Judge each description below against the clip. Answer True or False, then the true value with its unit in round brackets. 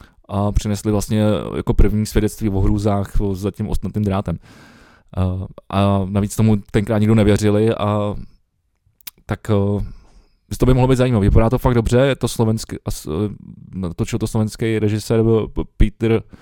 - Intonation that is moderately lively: False (1.9 semitones)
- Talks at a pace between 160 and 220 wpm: False (140 wpm)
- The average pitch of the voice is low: True (105 Hz)